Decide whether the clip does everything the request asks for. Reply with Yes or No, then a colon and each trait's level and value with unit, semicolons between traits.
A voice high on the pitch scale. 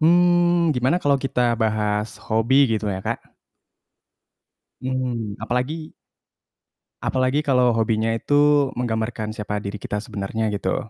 No: low, 120 Hz